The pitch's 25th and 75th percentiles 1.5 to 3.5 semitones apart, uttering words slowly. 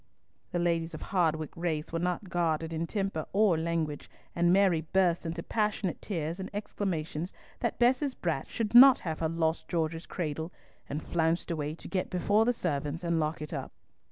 No: average, 3.1 semitones; average, 180 wpm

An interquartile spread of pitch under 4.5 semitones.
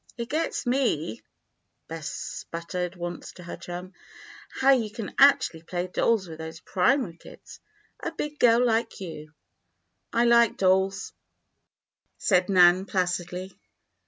No: average, 5.0 semitones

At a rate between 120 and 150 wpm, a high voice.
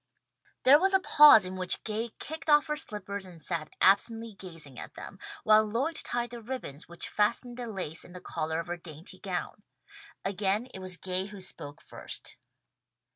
No: average, 185 wpm; high, 200 Hz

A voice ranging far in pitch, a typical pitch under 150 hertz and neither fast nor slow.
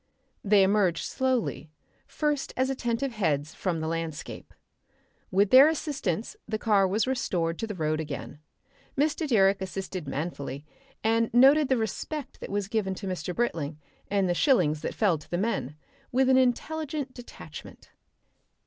No: wide, 7.3 semitones; high, 205 Hz; average, 150 wpm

